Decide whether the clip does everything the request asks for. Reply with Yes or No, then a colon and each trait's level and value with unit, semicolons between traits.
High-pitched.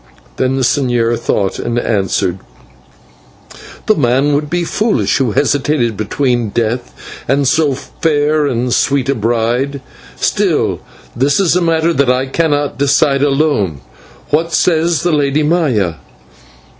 No: medium, 140 Hz